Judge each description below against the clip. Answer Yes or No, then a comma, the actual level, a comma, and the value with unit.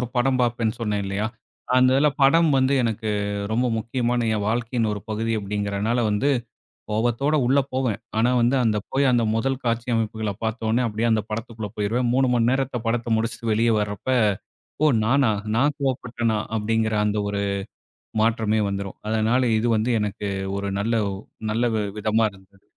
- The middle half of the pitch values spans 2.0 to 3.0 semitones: Yes, narrow, 2.4 semitones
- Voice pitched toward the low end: Yes, low, 115 Hz